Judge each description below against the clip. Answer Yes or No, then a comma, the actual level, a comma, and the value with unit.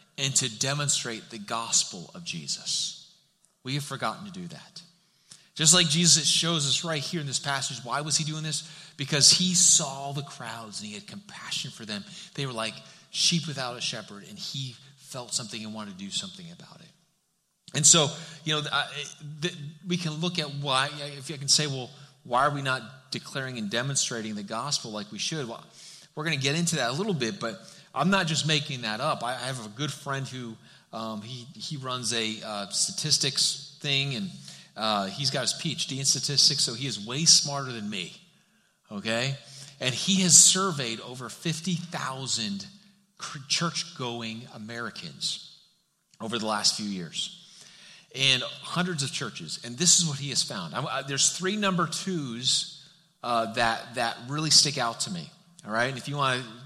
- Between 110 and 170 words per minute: No, average, 185 wpm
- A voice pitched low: No, medium, 145 Hz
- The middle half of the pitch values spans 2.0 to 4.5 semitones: No, average, 5.0 semitones